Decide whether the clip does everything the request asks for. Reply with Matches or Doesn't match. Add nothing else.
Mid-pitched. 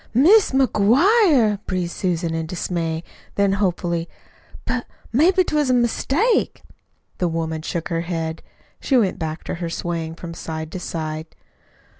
Matches